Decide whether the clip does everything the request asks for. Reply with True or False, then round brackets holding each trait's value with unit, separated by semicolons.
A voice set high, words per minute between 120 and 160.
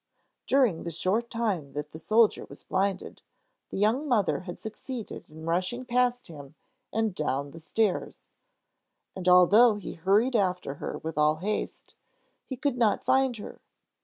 True (200 Hz; 155 wpm)